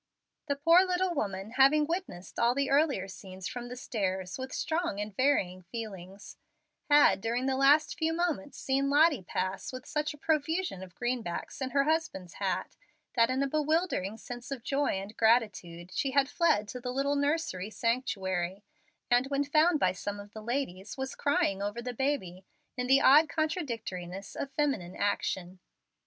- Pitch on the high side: Yes, very high, 250 Hz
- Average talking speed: Yes, average, 170 wpm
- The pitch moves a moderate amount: No, wide, 6.7 semitones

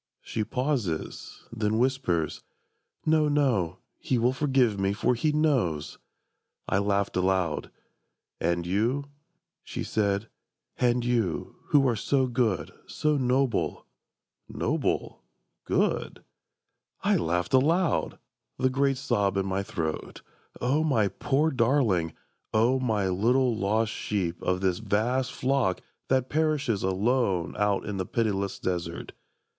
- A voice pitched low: Yes, low, 115 Hz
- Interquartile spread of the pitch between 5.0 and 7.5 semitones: Yes, wide, 5.4 semitones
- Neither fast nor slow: No, slow, 120 wpm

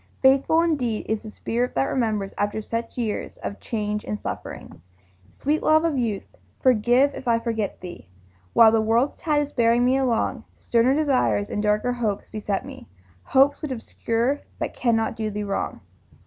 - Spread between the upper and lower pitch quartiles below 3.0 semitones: No, average, 3.8 semitones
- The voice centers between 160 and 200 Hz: No, high, 230 Hz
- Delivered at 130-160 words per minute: No, average, 170 wpm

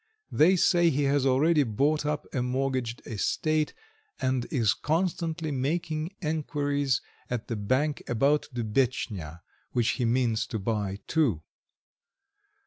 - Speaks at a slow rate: Yes, slow, 125 wpm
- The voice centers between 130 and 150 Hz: Yes, low, 135 Hz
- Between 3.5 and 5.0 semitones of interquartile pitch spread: Yes, average, 4.6 semitones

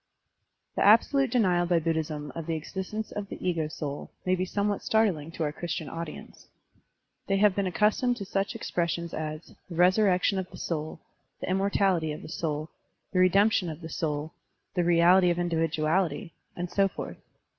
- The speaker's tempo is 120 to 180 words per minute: Yes, average, 170 wpm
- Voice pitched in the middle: Yes, medium, 175 Hz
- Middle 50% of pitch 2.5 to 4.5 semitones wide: Yes, average, 3.5 semitones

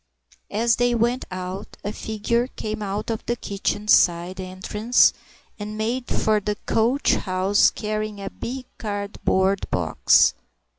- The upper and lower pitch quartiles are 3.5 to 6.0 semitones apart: No, narrow, 2.6 semitones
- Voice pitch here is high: Yes, high, 210 Hz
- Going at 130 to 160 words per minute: Yes, slow, 135 wpm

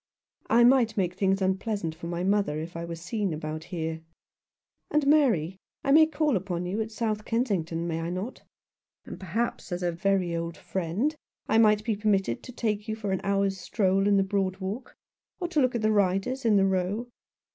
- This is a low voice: No, high, 195 Hz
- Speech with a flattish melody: No, average, 4.0 semitones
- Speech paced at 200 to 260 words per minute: Yes, fast, 205 wpm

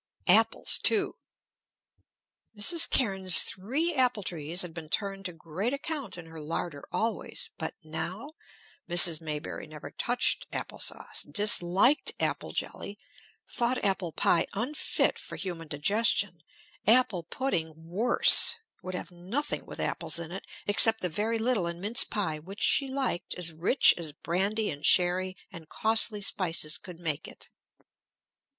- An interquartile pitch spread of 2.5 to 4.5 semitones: No, average, 5.1 semitones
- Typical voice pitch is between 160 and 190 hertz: Yes, medium, 185 Hz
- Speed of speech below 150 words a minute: Yes, average, 140 wpm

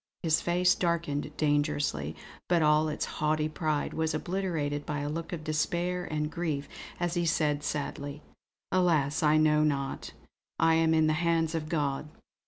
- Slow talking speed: No, average, 160 wpm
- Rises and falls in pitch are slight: Yes, narrow, 2.1 semitones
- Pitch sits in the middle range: Yes, medium, 155 Hz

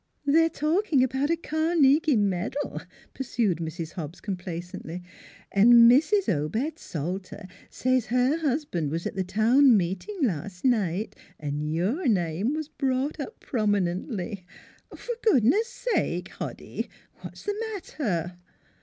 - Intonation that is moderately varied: No, wide, 8.6 semitones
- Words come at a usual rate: No, slow, 130 wpm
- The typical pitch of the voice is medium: No, high, 235 Hz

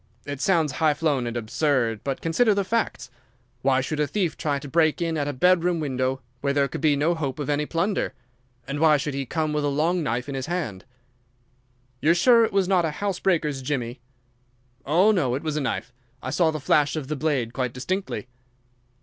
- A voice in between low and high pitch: Yes, medium, 150 Hz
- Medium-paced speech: No, fast, 215 wpm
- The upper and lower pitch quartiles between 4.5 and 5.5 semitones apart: No, average, 3.9 semitones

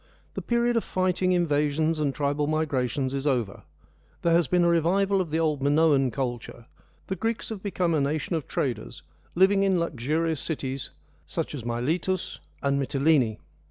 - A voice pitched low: No, medium, 155 Hz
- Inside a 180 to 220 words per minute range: No, average, 165 wpm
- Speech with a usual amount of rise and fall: Yes, average, 4.4 semitones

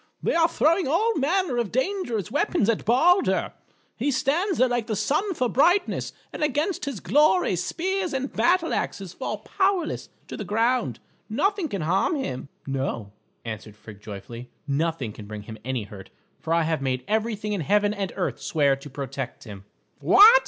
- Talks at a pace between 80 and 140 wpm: No, average, 175 wpm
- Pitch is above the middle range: Yes, high, 220 Hz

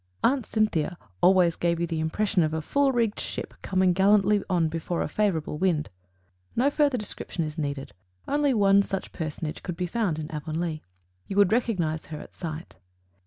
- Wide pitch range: No, average, 4.8 semitones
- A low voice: No, medium, 180 Hz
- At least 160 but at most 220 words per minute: Yes, average, 175 wpm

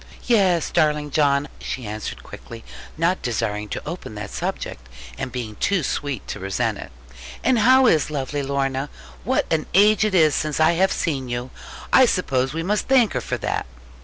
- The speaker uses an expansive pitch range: Yes, wide, 6.7 semitones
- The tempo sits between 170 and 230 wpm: Yes, average, 180 wpm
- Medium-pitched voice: Yes, medium, 150 Hz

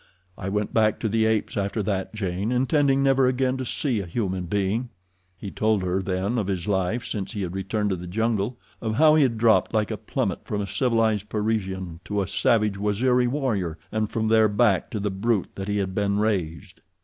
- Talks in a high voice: No, low, 105 Hz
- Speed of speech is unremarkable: No, fast, 210 wpm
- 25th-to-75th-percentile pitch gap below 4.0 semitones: Yes, average, 3.0 semitones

